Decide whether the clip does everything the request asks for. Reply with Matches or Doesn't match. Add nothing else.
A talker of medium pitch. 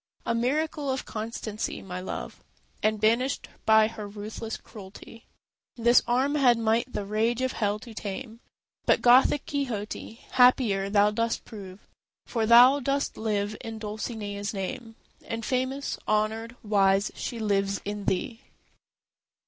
Doesn't match